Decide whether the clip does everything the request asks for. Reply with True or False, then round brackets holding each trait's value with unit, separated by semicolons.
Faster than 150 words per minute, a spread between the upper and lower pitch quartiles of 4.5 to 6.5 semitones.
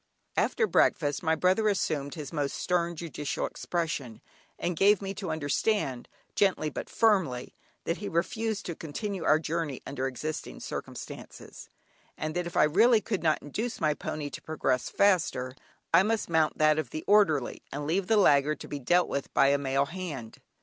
True (175 wpm; 4.9 semitones)